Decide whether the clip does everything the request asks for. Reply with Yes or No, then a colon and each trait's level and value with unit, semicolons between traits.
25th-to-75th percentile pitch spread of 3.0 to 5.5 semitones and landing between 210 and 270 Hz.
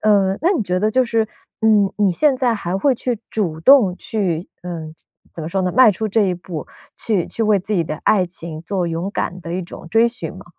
No: average, 4.1 semitones; high, 195 Hz